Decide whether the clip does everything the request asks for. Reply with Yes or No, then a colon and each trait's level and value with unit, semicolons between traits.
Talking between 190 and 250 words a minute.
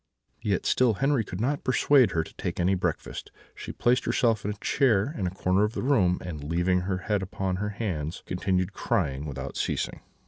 Yes: average, 200 wpm